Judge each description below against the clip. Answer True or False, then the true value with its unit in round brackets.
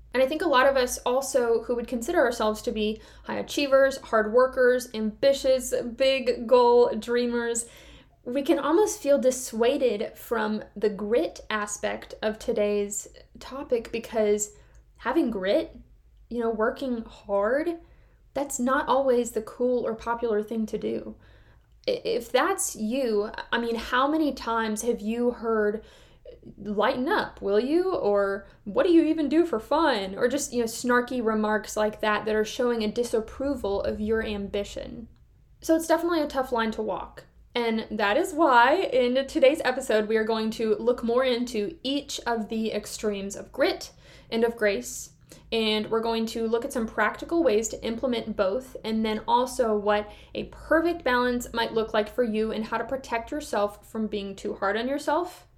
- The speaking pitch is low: False (235 Hz)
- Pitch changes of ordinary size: True (3.6 semitones)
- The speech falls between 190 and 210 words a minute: False (170 wpm)